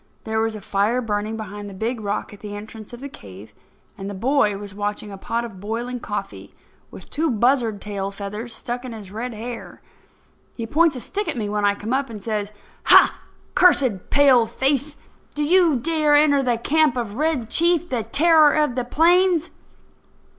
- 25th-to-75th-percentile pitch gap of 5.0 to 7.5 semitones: Yes, wide, 5.5 semitones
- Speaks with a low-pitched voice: No, high, 235 Hz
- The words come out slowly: No, average, 190 wpm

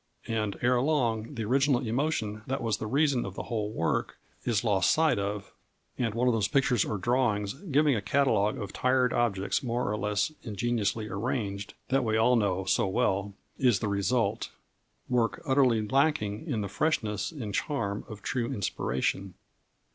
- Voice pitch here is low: Yes, low, 115 Hz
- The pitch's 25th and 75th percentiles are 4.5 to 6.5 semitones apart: No, average, 3.9 semitones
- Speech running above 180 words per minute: No, average, 170 wpm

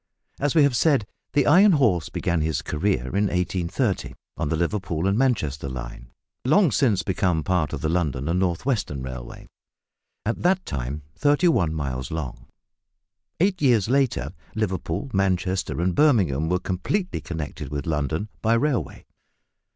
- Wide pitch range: Yes, wide, 8.4 semitones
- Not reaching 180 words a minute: Yes, average, 150 wpm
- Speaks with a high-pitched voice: No, very low, 90 Hz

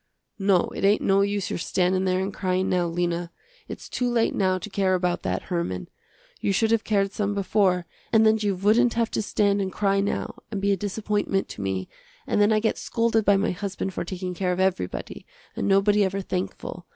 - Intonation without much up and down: Yes, narrow, 2.1 semitones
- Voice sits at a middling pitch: No, high, 195 Hz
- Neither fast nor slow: No, fast, 210 wpm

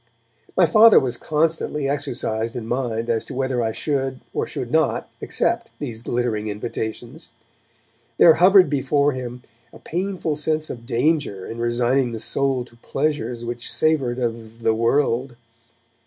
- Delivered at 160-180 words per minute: No, average, 145 wpm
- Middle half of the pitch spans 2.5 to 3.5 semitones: No, average, 3.9 semitones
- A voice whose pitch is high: No, low, 125 Hz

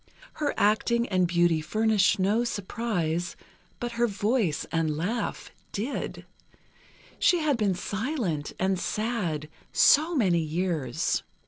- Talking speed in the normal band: No, slow, 115 wpm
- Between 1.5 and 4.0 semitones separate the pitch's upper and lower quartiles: No, wide, 5.4 semitones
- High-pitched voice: Yes, high, 200 Hz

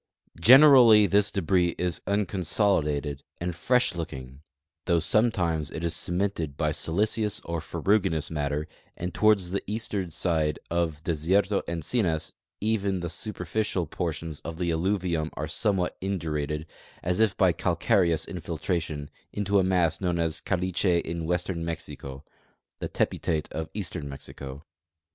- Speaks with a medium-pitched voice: No, very low, 85 Hz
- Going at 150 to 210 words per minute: No, slow, 135 wpm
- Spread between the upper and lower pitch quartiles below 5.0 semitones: Yes, average, 3.6 semitones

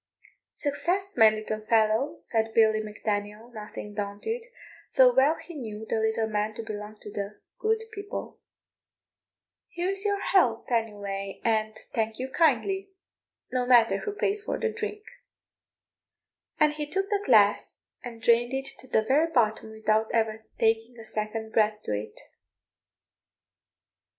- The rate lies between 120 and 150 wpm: Yes, average, 145 wpm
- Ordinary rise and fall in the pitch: No, wide, 5.9 semitones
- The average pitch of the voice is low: No, high, 225 Hz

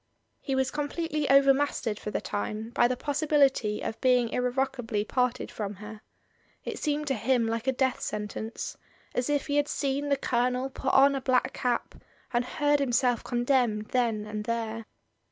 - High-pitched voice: Yes, very high, 250 Hz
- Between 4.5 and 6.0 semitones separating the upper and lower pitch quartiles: No, average, 3.5 semitones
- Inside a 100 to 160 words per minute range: No, average, 170 wpm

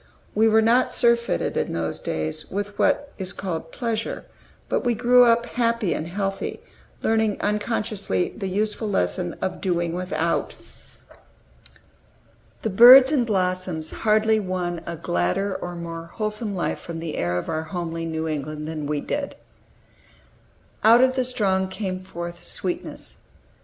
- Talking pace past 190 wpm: No, average, 145 wpm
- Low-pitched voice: No, high, 190 Hz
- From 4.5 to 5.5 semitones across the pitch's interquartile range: Yes, average, 5.0 semitones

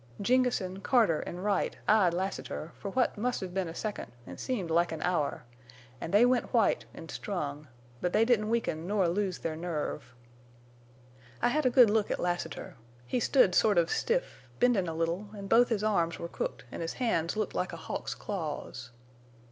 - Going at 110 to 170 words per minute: No, average, 190 wpm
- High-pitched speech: Yes, high, 195 Hz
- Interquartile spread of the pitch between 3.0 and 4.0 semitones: No, average, 4.8 semitones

